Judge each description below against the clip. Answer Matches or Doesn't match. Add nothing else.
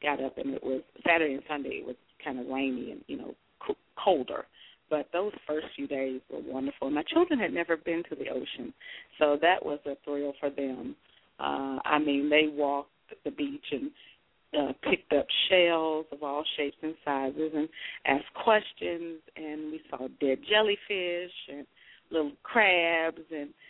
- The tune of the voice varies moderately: Matches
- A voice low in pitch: Doesn't match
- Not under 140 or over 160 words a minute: Doesn't match